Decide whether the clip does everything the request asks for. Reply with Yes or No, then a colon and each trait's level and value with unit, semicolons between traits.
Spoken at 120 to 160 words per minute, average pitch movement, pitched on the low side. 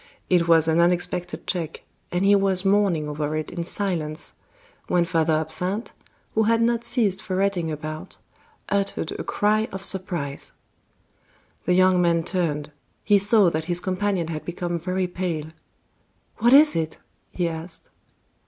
No: average, 145 wpm; average, 3.3 semitones; medium, 180 Hz